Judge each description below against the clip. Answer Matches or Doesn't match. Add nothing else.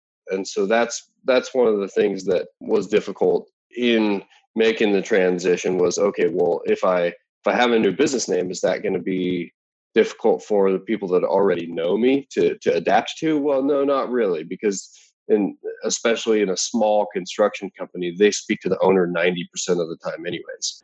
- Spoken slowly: Doesn't match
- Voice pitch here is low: Matches